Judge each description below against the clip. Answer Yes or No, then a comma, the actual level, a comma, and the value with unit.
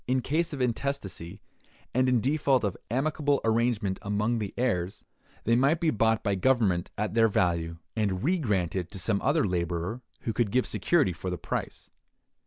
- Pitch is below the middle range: Yes, low, 115 Hz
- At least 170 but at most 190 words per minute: Yes, average, 175 wpm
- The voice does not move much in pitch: No, wide, 5.5 semitones